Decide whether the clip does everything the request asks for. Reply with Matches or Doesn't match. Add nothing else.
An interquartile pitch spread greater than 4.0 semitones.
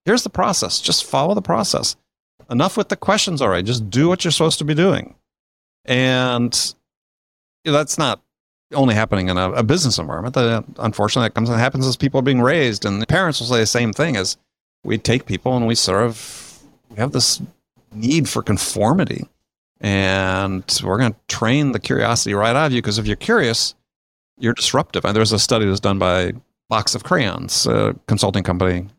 Matches